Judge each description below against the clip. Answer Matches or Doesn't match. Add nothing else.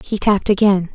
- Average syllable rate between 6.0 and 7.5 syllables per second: Matches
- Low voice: Doesn't match